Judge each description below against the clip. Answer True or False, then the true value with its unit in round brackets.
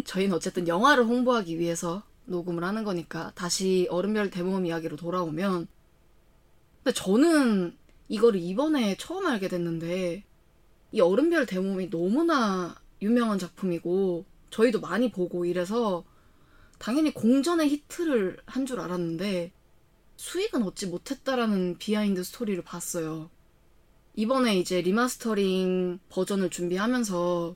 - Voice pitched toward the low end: False (190 Hz)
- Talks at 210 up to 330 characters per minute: True (305 characters per minute)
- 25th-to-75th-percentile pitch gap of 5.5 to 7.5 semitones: False (5.1 semitones)